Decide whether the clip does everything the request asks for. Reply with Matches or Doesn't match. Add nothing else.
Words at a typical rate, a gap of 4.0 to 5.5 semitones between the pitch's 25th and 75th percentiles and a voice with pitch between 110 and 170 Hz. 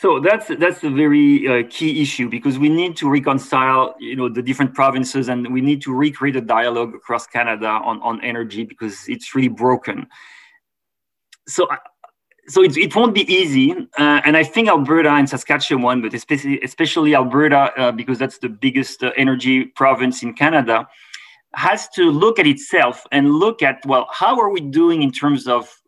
Doesn't match